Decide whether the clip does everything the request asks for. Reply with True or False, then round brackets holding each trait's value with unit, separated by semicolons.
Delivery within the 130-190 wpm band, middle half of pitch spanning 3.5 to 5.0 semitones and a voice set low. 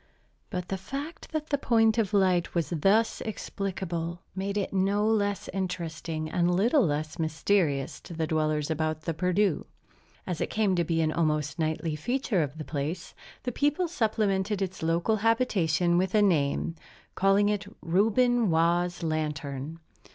False (155 wpm; 4.6 semitones; 180 Hz)